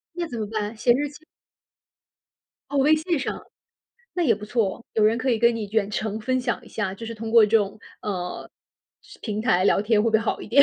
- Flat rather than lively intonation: No, average, 3.2 semitones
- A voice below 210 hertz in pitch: No, high, 225 Hz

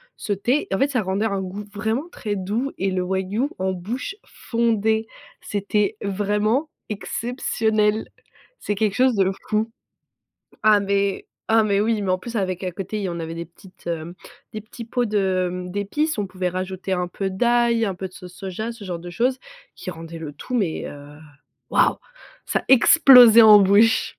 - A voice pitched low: No, high, 205 Hz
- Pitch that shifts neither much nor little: Yes, average, 3.3 semitones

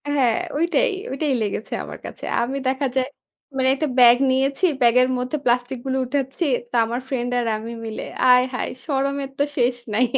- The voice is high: Yes, very high, 260 Hz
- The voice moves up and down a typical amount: No, narrow, 2.2 semitones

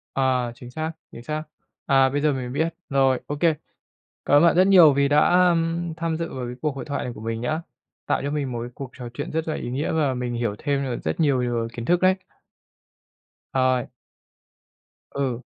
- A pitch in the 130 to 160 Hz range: Yes, medium, 140 Hz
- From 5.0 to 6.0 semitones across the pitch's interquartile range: No, average, 4.2 semitones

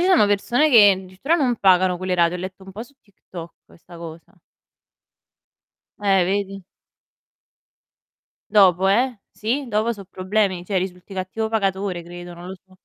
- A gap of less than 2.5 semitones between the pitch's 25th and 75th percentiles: No, average, 2.9 semitones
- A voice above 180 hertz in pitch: Yes, high, 190 Hz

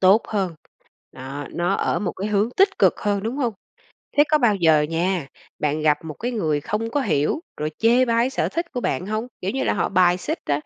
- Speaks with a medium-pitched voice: No, high, 195 Hz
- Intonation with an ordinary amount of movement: No, wide, 6.5 semitones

